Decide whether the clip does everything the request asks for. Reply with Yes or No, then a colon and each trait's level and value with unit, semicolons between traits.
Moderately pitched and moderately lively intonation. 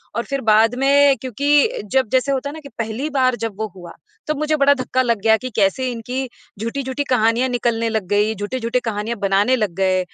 No: high, 245 Hz; average, 3.5 semitones